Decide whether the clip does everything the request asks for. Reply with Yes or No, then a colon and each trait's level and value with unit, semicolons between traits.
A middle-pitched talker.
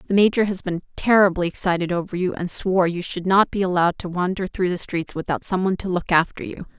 Yes: medium, 180 Hz